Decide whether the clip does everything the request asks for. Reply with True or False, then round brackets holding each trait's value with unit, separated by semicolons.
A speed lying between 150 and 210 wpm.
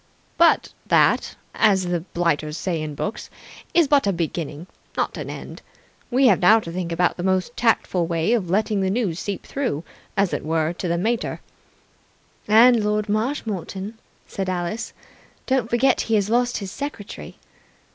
True (165 wpm)